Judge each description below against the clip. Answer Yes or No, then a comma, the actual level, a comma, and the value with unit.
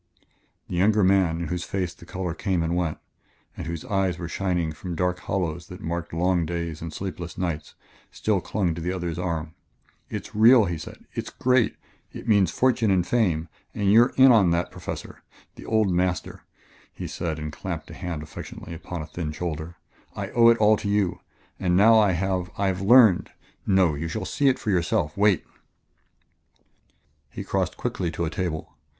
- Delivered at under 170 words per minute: No, average, 185 wpm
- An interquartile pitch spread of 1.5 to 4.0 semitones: Yes, average, 3.1 semitones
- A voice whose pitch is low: Yes, very low, 90 Hz